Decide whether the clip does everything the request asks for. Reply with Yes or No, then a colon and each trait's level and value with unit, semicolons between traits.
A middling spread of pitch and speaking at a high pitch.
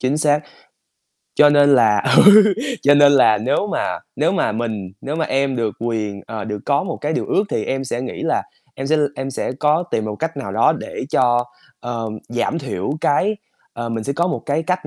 No: average, 4.7 semitones; low, 135 Hz